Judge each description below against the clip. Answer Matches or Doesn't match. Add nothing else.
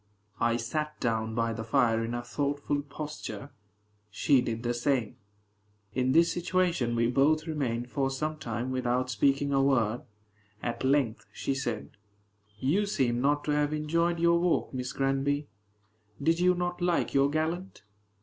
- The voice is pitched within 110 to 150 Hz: Matches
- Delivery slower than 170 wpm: Matches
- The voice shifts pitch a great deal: Doesn't match